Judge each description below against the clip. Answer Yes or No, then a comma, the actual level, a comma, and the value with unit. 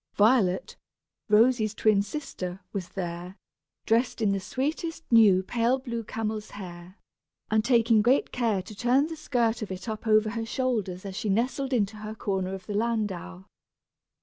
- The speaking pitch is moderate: No, high, 215 Hz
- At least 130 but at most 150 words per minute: No, average, 160 wpm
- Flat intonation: No, average, 3.5 semitones